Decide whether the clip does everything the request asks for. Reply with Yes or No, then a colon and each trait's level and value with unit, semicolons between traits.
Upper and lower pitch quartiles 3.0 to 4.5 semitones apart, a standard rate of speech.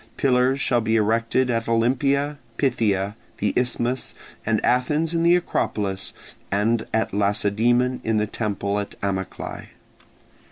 No: average, 3.6 semitones; slow, 125 wpm